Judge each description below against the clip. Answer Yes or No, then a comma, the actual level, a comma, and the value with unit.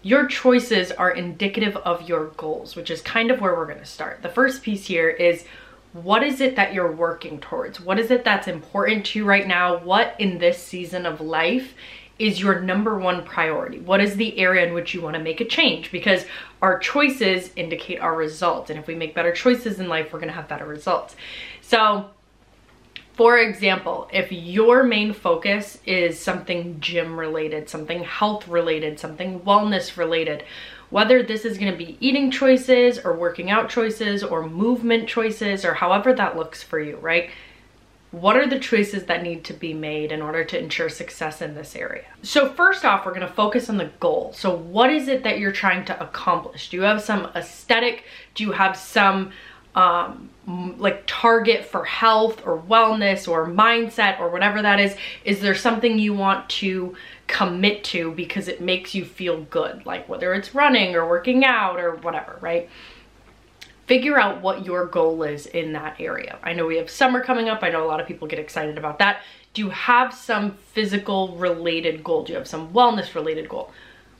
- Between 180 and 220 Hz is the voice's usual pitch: Yes, high, 190 Hz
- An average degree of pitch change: Yes, average, 4.5 semitones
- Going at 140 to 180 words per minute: No, average, 195 wpm